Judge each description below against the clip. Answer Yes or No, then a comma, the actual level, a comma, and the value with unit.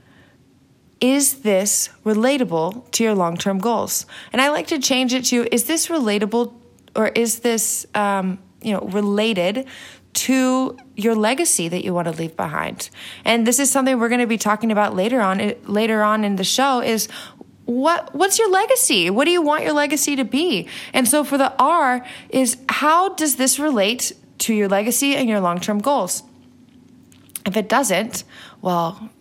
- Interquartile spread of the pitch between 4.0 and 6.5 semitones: Yes, average, 4.5 semitones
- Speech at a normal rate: Yes, average, 175 wpm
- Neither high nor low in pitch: No, high, 235 Hz